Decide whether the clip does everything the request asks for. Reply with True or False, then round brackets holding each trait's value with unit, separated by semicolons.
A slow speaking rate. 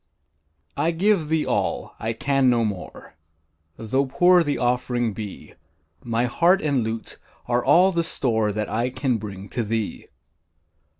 False (145 wpm)